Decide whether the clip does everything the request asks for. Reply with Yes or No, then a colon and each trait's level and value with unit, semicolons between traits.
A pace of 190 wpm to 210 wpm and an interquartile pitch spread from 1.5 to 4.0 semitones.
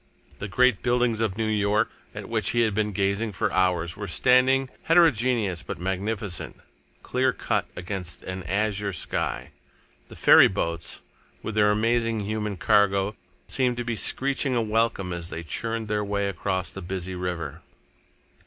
No: average, 155 wpm; average, 3.5 semitones